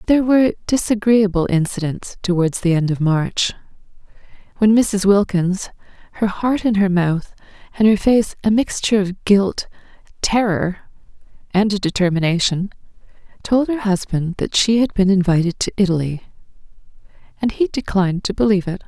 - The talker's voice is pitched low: No, high, 195 Hz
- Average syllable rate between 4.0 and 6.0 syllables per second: Yes, 5.1 syllables/s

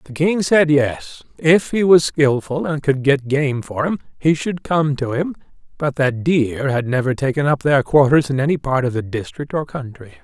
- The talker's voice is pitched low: No, medium, 145 Hz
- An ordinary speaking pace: No, fast, 210 wpm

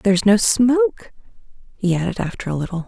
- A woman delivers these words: Yes, female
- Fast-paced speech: No, average, 165 wpm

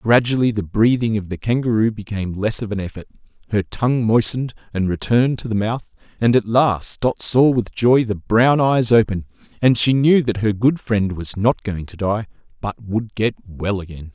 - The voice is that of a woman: No, male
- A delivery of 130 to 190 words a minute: No, average, 200 wpm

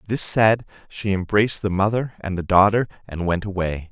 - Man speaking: Yes, male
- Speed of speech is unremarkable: Yes, average, 185 wpm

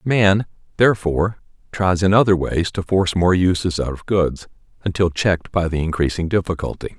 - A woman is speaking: No, male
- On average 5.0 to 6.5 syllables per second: Yes, 5.5 syllables/s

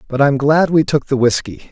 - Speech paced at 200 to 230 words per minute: No, fast, 245 wpm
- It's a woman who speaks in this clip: No, male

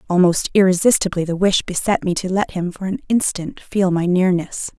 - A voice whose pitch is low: No, medium, 185 Hz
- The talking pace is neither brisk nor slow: Yes, average, 190 wpm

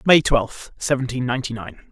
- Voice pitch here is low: Yes, low, 125 Hz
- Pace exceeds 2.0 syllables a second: No, 1.7 syllables/s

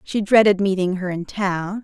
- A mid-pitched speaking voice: No, high, 195 Hz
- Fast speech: No, average, 195 wpm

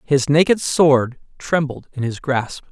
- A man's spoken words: Yes, male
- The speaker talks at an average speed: Yes, average, 155 wpm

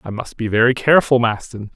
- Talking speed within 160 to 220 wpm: Yes, fast, 205 wpm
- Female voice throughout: No, male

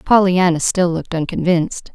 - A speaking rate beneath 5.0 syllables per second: No, 5.4 syllables/s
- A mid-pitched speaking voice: Yes, medium, 175 Hz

